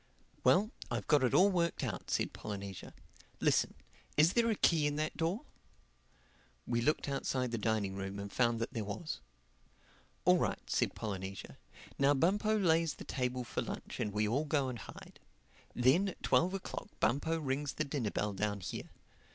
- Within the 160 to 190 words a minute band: Yes, average, 175 wpm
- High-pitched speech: No, low, 135 Hz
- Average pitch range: No, wide, 7.2 semitones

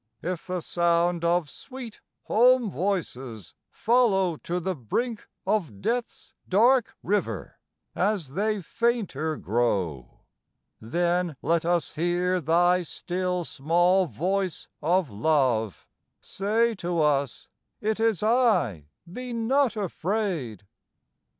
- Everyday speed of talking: No, slow, 105 wpm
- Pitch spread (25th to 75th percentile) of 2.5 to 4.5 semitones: No, wide, 5.6 semitones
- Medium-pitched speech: Yes, medium, 180 Hz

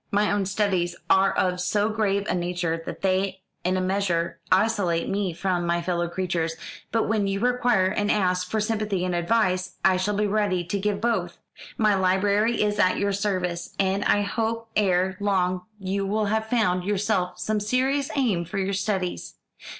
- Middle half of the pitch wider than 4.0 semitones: No, narrow, 2.4 semitones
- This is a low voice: No, high, 195 Hz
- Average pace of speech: Yes, average, 180 wpm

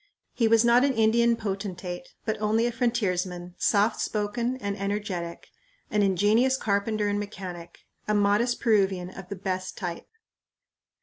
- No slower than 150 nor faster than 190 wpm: No, average, 140 wpm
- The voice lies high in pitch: Yes, high, 205 Hz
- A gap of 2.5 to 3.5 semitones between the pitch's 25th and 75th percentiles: Yes, average, 3.2 semitones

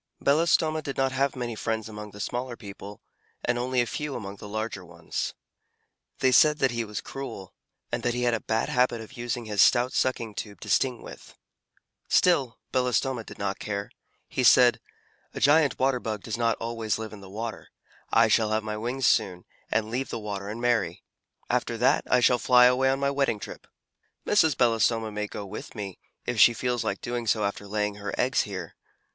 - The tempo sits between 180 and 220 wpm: Yes, average, 200 wpm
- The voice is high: No, low, 115 Hz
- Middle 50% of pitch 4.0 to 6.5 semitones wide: No, average, 3.2 semitones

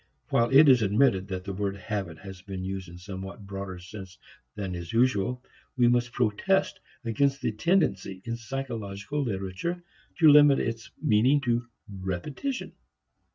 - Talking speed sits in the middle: Yes, average, 155 wpm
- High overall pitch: No, low, 105 Hz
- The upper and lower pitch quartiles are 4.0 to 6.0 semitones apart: Yes, average, 5.2 semitones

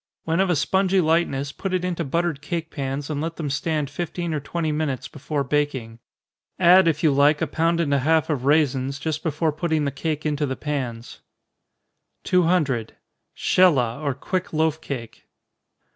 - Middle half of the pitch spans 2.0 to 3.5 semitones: Yes, average, 3.1 semitones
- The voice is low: No, medium, 155 Hz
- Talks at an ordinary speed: Yes, average, 175 wpm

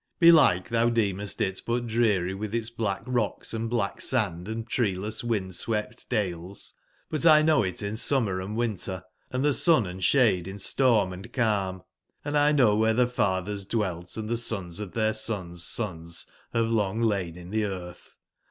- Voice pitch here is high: No, low, 105 Hz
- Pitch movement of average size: Yes, average, 3.9 semitones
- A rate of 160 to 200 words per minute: Yes, average, 170 wpm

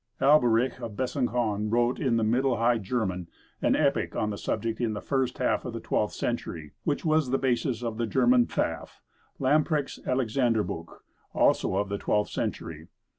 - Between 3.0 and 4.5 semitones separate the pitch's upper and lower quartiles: Yes, average, 3.5 semitones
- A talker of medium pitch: No, low, 120 Hz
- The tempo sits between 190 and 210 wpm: No, average, 165 wpm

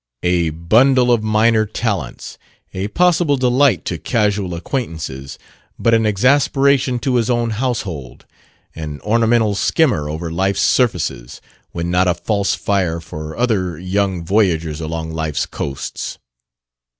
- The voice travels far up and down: Yes, wide, 6.2 semitones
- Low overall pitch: Yes, low, 100 Hz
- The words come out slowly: Yes, slow, 125 wpm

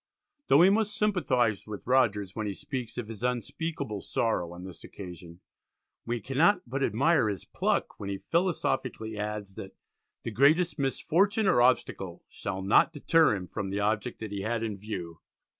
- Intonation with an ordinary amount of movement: No, wide, 5.9 semitones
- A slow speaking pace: No, average, 170 wpm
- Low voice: Yes, low, 110 Hz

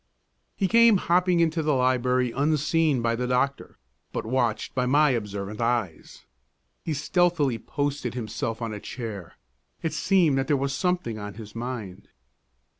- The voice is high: No, low, 130 Hz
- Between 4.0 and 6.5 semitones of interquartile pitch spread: Yes, average, 5.1 semitones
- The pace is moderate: Yes, average, 150 wpm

